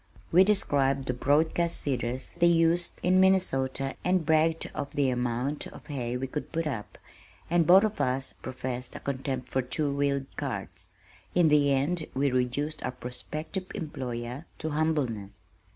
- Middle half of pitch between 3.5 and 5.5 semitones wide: Yes, average, 4.1 semitones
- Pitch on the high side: No, medium, 140 Hz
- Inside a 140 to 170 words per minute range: Yes, average, 155 wpm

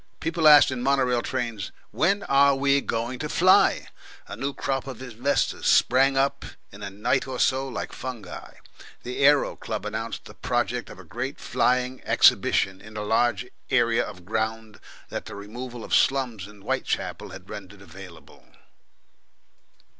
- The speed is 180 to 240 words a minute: No, average, 160 wpm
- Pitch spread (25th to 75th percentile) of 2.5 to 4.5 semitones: Yes, average, 4.0 semitones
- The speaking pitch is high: No, low, 120 Hz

